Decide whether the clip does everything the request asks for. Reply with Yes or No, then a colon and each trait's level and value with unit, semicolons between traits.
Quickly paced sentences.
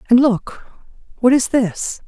No: average, 145 wpm